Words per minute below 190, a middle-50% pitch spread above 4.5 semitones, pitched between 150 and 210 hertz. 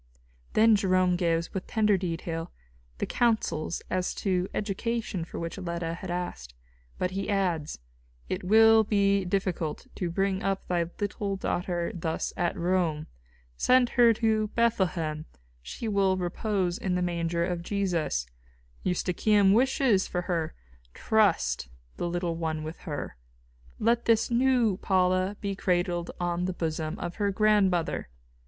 No: average, 140 wpm; average, 3.2 semitones; medium, 185 Hz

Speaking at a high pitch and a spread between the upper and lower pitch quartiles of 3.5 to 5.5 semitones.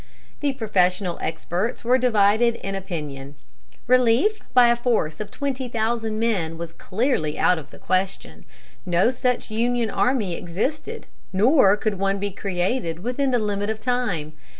Yes: high, 215 Hz; average, 5.2 semitones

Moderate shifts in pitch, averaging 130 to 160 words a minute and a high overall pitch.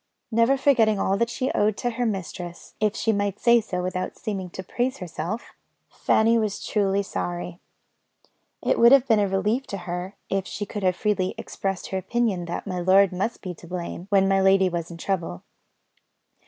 No: average, 3.4 semitones; average, 190 wpm; high, 195 Hz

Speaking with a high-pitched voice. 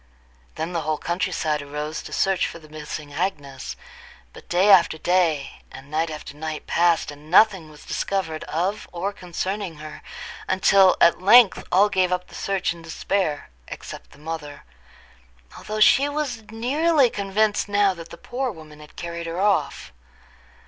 No: medium, 175 Hz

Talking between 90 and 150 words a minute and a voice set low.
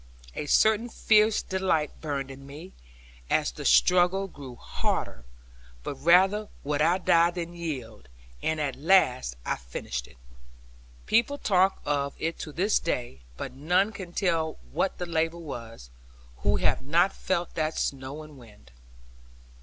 No: average, 145 wpm; medium, 160 Hz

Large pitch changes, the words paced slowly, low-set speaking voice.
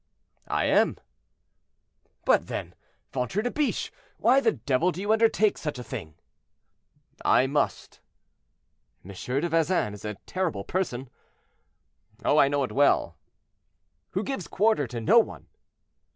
No: wide, 8.2 semitones; slow, 130 wpm; medium, 150 Hz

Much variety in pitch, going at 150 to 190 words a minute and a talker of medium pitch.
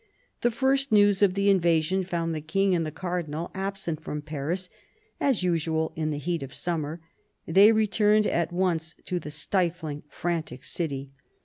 No: average, 3.7 semitones; average, 165 wpm; medium, 175 Hz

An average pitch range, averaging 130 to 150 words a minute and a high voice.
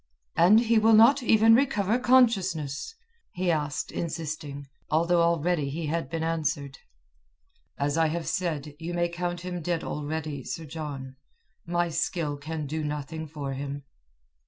No: average, 3.1 semitones; average, 145 wpm; medium, 165 Hz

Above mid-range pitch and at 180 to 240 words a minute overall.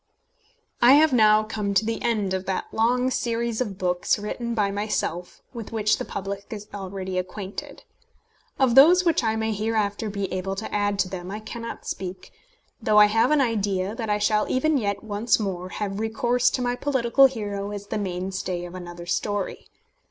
Yes: high, 210 Hz; average, 185 wpm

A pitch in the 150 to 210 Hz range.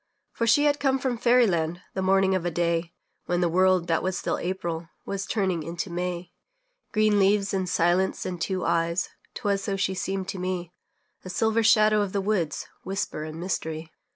Yes: medium, 185 Hz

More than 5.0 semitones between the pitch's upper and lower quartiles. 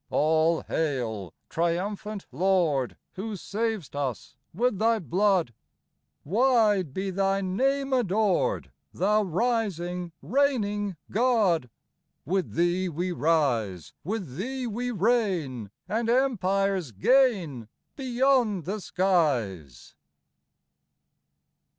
Yes: wide, 5.5 semitones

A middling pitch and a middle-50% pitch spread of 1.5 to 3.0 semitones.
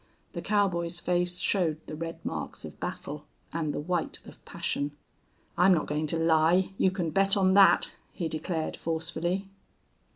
Yes: medium, 170 Hz; narrow, 2.6 semitones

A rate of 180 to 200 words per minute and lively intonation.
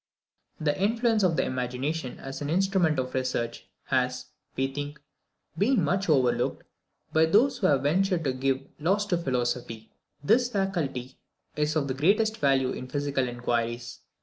No: average, 150 wpm; wide, 6.4 semitones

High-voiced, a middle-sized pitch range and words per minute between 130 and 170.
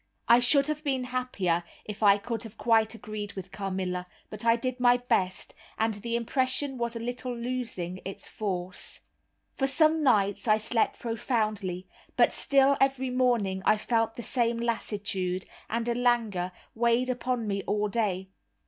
Yes: high, 230 Hz; average, 3.7 semitones; average, 160 wpm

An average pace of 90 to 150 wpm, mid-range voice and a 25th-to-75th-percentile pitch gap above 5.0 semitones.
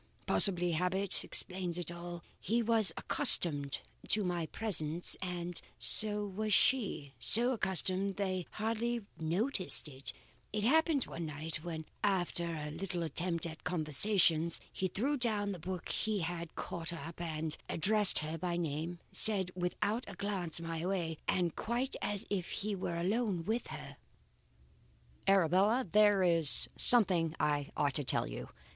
No: average, 145 wpm; medium, 180 Hz; average, 3.9 semitones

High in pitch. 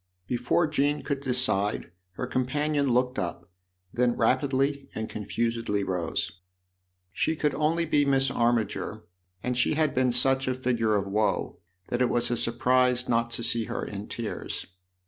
No: low, 125 Hz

